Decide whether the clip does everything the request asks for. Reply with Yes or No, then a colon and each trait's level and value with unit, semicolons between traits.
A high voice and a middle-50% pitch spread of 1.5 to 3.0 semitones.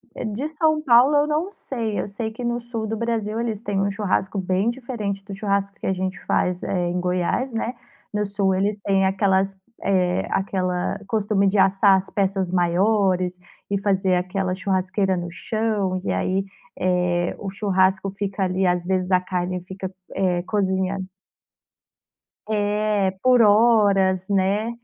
Yes: high, 195 Hz; narrow, 2.4 semitones